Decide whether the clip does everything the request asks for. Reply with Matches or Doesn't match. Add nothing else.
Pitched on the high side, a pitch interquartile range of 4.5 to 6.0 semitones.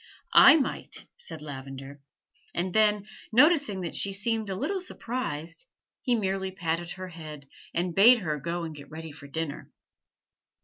Doesn't match